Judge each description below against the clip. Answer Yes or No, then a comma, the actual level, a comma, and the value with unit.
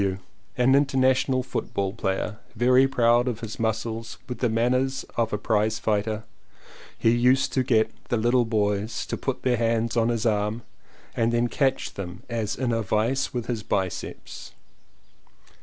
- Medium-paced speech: Yes, average, 165 wpm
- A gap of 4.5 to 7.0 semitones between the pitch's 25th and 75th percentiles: No, narrow, 2.4 semitones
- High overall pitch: No, low, 115 Hz